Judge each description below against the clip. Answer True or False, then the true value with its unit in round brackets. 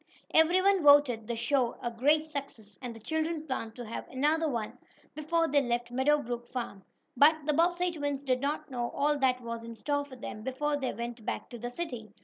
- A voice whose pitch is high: True (265 Hz)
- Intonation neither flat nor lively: True (4.0 semitones)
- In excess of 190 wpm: True (205 wpm)